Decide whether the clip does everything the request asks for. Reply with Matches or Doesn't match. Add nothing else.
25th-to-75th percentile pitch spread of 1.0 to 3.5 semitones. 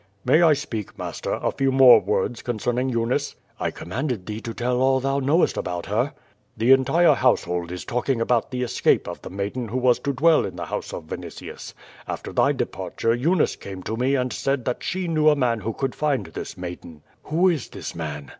Doesn't match